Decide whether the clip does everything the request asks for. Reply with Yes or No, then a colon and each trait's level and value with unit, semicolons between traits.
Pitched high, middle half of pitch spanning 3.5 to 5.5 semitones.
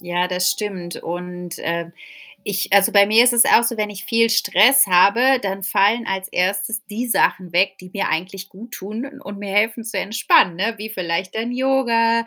Yes: high, 200 Hz; average, 3.8 semitones